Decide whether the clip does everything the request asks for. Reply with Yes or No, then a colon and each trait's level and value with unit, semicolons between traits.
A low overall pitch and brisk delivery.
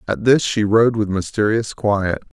No: low, 105 Hz; average, 175 wpm